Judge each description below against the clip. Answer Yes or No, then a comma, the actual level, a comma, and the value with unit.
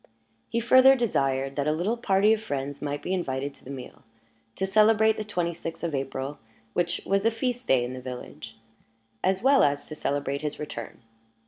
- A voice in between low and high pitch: Yes, medium, 165 Hz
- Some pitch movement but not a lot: No, wide, 7.7 semitones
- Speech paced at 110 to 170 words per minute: No, average, 195 wpm